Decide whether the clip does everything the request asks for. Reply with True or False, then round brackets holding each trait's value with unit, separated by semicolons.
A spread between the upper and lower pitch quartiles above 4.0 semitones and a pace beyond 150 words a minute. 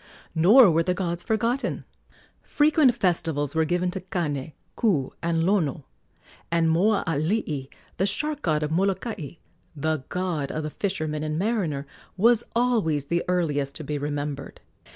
False (4.8 semitones; 140 wpm)